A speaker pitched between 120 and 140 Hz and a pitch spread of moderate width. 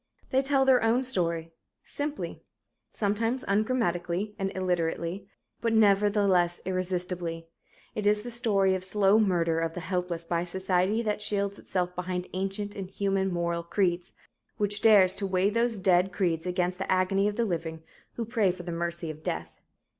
No: high, 190 Hz; average, 3.0 semitones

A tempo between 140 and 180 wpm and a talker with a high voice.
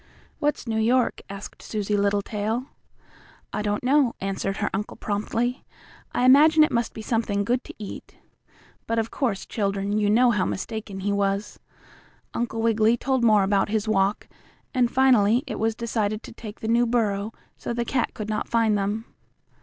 Yes: average, 170 wpm; high, 220 Hz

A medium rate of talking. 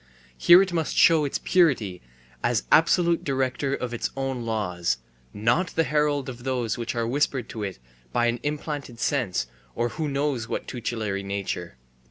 Yes: average, 165 wpm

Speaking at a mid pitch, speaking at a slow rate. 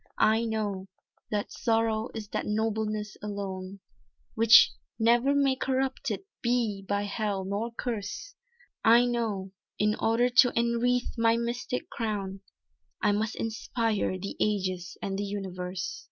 No: high, 220 Hz; slow, 125 wpm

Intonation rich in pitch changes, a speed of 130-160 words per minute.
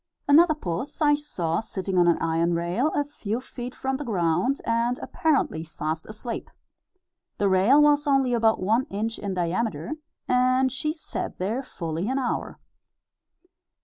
Yes: wide, 7.0 semitones; average, 150 wpm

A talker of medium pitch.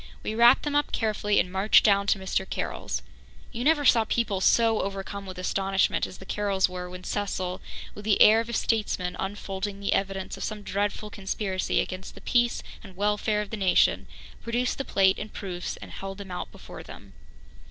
No: high, 200 Hz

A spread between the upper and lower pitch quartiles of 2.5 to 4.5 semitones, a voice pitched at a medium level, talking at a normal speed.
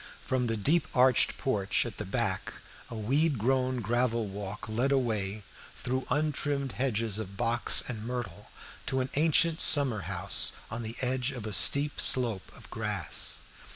No: average, 3.5 semitones; low, 120 Hz; average, 155 wpm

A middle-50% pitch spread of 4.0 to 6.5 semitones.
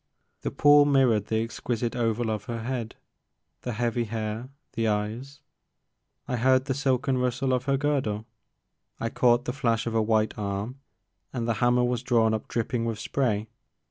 No: average, 2.7 semitones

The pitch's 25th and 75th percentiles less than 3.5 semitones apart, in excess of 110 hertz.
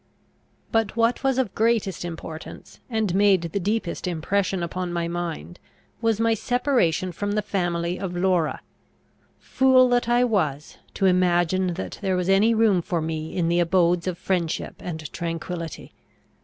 No: average, 4.2 semitones; medium, 185 Hz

